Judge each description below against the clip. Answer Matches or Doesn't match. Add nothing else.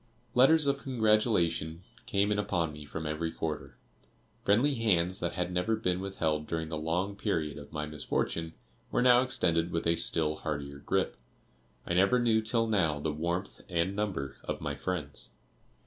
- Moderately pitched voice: Doesn't match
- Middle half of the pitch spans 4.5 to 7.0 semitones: Matches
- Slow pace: Doesn't match